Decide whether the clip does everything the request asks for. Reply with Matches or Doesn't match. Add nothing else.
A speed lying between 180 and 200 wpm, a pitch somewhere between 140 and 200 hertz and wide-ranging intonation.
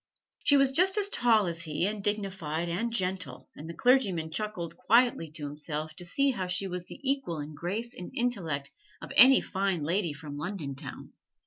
Matches